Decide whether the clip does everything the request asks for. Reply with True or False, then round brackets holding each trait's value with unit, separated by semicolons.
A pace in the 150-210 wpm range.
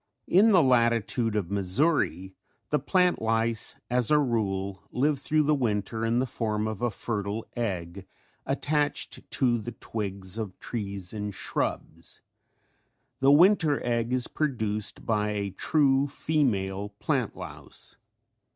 False (135 wpm)